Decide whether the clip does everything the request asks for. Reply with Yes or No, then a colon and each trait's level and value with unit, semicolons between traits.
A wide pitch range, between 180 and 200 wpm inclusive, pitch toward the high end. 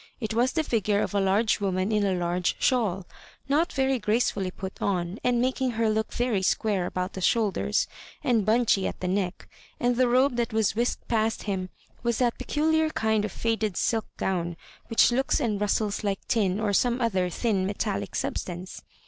No: average, 3.8 semitones; average, 185 wpm; high, 215 Hz